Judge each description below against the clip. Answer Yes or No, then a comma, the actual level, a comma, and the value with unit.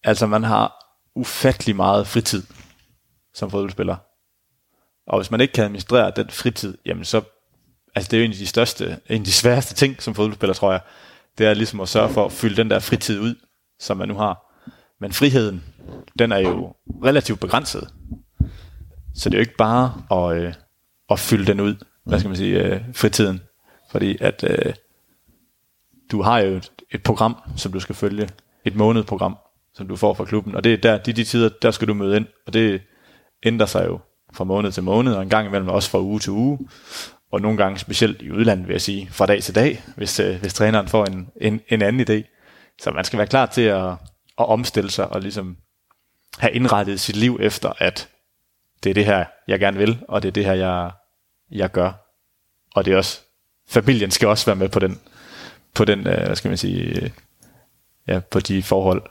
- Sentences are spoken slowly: No, average, 200 wpm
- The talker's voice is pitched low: Yes, low, 105 Hz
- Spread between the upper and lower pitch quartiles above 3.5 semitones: No, average, 2.9 semitones